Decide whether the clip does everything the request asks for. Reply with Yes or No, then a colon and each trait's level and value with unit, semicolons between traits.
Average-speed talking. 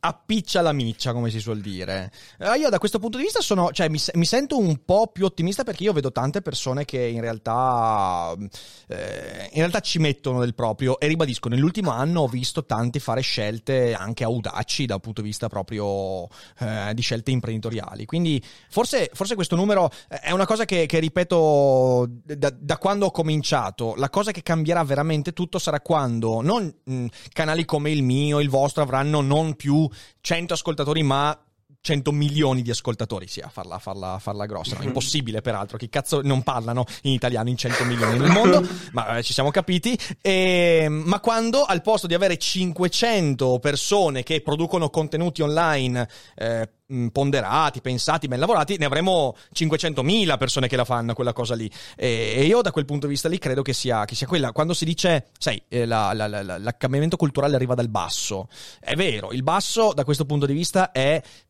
No: fast, 180 wpm